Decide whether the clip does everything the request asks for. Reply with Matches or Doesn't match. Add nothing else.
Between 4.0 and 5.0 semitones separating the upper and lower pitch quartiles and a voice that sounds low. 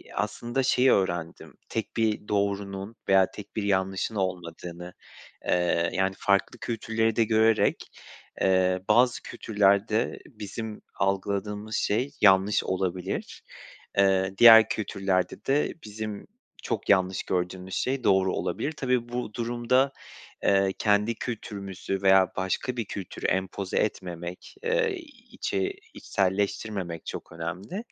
Doesn't match